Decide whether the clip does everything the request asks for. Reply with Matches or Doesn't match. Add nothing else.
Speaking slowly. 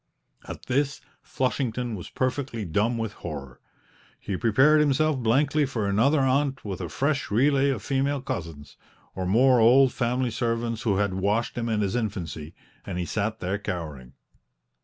Doesn't match